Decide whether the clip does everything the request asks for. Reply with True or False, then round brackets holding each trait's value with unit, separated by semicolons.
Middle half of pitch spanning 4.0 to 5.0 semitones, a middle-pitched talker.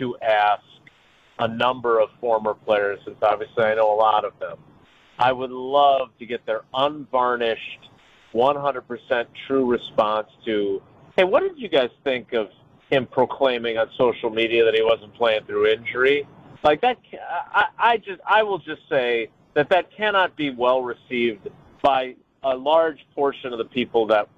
False (4.5 semitones; 125 Hz)